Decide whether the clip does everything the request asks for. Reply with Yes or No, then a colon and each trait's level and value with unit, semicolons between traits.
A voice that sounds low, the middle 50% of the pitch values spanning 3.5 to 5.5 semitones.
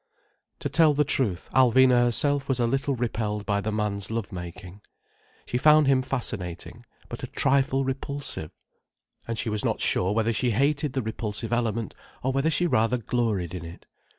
Yes: low, 120 Hz; average, 4.3 semitones